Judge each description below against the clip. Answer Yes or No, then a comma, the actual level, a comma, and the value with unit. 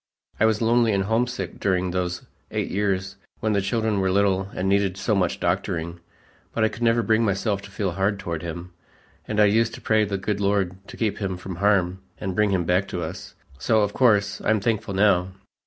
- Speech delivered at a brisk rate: Yes, fast, 210 wpm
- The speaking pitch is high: No, low, 100 Hz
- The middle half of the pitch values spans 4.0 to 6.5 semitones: No, narrow, 2.5 semitones